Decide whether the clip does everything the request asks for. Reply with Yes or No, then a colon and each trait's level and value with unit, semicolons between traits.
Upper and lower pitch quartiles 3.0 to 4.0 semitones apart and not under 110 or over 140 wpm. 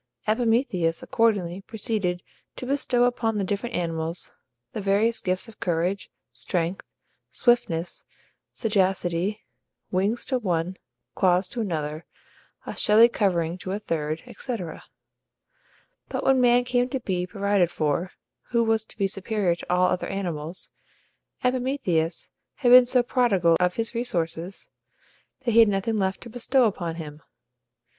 No: average, 5.0 semitones; slow, 135 wpm